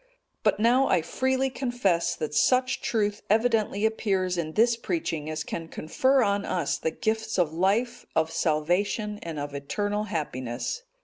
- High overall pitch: Yes, high, 205 Hz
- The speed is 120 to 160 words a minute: Yes, average, 150 wpm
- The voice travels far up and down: Yes, wide, 6.4 semitones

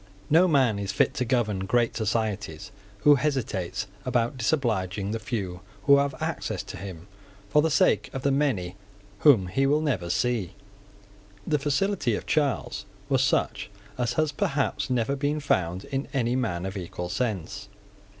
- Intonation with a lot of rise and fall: Yes, wide, 6.2 semitones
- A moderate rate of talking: Yes, average, 160 wpm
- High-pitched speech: No, low, 120 Hz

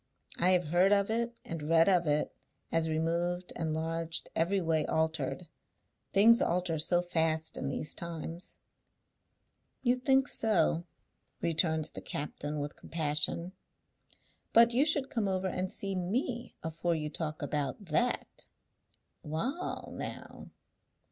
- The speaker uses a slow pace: Yes, slow, 130 wpm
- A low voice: No, medium, 170 Hz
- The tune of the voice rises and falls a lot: No, average, 3.6 semitones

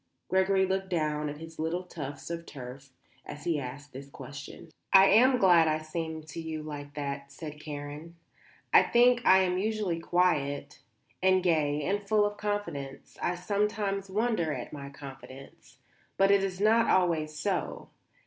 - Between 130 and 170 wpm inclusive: Yes, average, 160 wpm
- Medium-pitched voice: Yes, medium, 165 Hz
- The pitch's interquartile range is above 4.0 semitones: Yes, average, 4.8 semitones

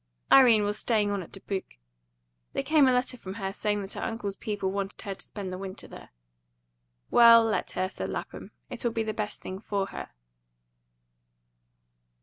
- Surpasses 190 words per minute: No, average, 175 wpm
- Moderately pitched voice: No, high, 205 Hz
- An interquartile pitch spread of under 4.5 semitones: Yes, average, 2.7 semitones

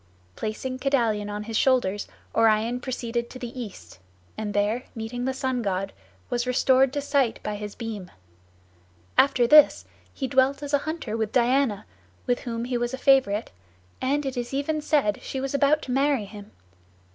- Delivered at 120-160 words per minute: No, average, 170 wpm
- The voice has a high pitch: Yes, high, 245 Hz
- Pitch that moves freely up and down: No, average, 3.7 semitones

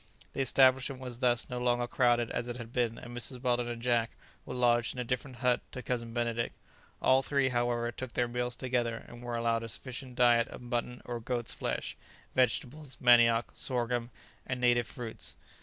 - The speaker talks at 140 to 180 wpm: No, average, 190 wpm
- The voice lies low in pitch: Yes, low, 120 Hz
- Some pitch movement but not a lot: No, narrow, 1.1 semitones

